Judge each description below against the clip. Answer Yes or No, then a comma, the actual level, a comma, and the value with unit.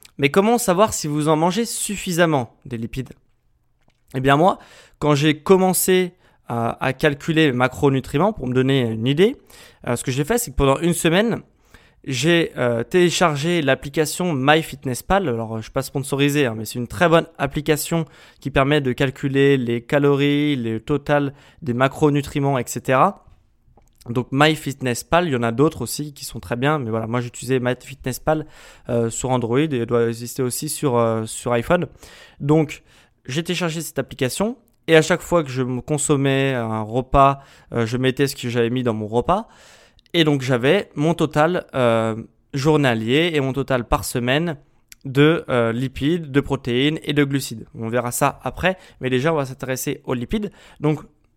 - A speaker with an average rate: Yes, average, 170 wpm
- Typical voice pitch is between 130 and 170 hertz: Yes, medium, 140 Hz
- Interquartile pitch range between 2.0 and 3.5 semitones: No, average, 4.0 semitones